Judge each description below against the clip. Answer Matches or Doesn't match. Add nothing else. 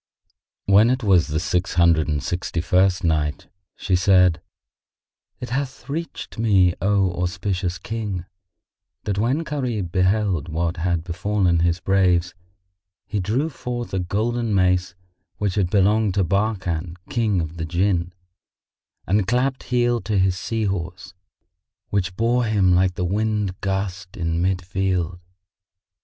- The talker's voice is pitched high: Doesn't match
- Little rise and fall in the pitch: Doesn't match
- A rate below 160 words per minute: Matches